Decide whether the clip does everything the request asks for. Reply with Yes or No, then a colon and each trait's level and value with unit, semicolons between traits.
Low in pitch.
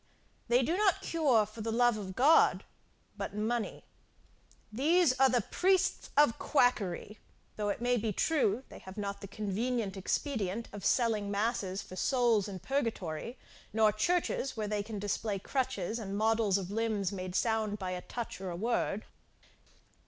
No: high, 220 Hz